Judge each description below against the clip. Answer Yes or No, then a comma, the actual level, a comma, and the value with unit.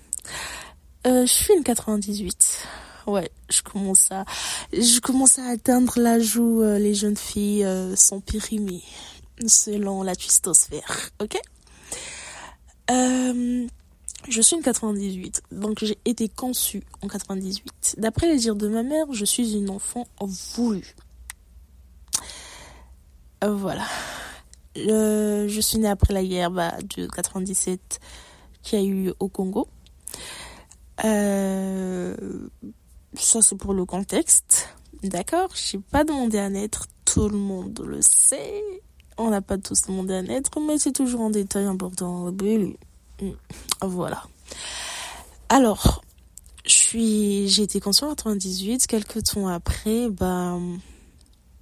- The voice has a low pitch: No, high, 205 Hz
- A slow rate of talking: Yes, slow, 125 wpm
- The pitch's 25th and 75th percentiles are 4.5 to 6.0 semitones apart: No, average, 3.6 semitones